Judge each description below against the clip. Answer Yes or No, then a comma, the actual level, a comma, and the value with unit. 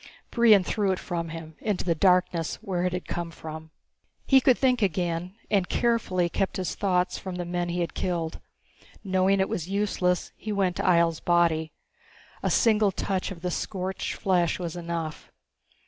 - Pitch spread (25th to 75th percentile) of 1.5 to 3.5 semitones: Yes, narrow, 2.4 semitones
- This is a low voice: No, medium, 180 Hz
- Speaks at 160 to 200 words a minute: Yes, average, 180 wpm